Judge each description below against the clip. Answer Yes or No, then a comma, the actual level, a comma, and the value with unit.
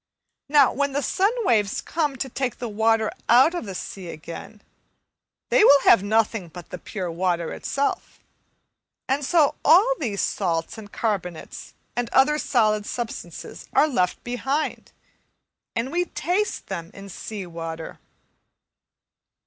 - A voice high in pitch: Yes, high, 225 Hz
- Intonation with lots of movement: Yes, wide, 6.8 semitones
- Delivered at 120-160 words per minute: Yes, average, 140 wpm